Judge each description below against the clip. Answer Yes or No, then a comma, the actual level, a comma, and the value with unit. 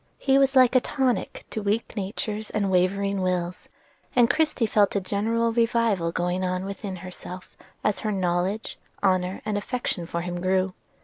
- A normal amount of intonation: Yes, average, 3.8 semitones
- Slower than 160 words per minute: No, average, 165 wpm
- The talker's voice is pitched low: No, high, 200 Hz